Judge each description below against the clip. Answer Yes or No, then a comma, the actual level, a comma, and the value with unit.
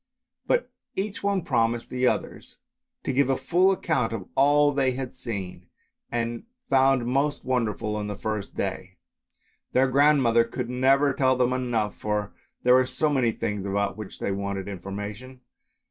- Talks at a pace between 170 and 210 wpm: No, average, 160 wpm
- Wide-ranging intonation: No, average, 4.2 semitones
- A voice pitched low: Yes, low, 125 Hz